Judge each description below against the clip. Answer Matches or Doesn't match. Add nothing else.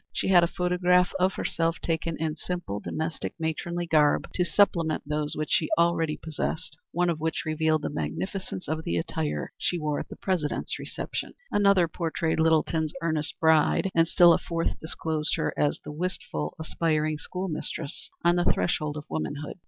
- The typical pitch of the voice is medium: Matches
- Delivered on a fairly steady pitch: Matches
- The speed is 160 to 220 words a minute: Matches